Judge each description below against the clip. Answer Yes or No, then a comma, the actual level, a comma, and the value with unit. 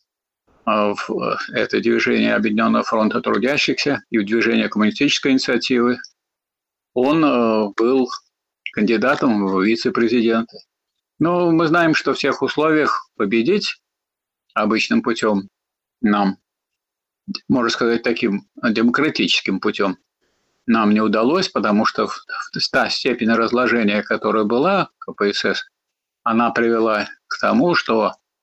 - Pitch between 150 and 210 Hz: No, low, 115 Hz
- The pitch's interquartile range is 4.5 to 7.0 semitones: No, average, 3.1 semitones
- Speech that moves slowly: Yes, slow, 105 wpm